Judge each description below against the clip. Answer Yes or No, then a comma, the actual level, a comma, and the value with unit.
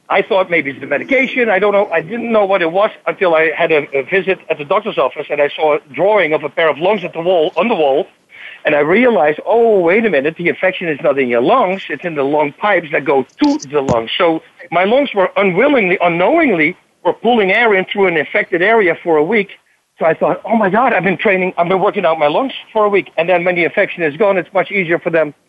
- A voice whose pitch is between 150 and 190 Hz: Yes, medium, 185 Hz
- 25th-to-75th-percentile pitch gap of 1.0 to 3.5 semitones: No, average, 4.3 semitones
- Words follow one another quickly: Yes, fast, 265 wpm